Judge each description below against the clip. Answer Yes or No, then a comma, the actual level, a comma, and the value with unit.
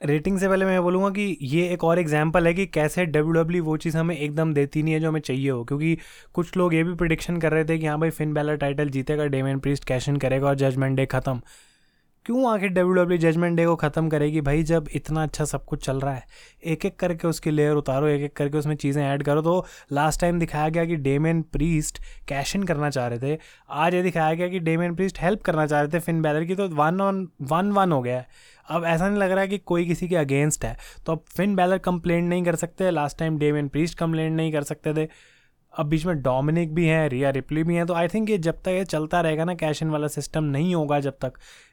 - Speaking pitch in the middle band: Yes, medium, 160 Hz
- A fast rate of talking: Yes, fast, 260 wpm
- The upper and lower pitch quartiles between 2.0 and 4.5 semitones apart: Yes, average, 2.8 semitones